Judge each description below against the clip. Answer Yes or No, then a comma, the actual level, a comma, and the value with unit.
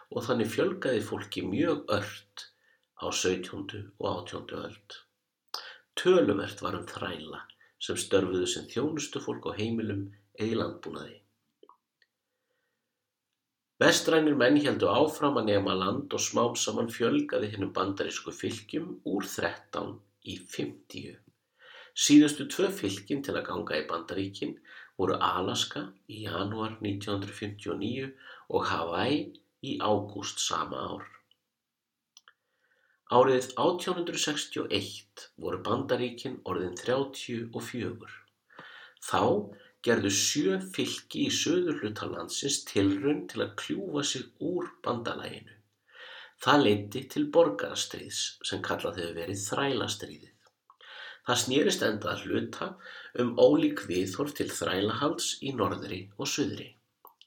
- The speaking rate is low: Yes, slow, 110 wpm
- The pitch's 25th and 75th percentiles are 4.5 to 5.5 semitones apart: Yes, average, 5.1 semitones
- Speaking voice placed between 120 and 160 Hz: No, low, 105 Hz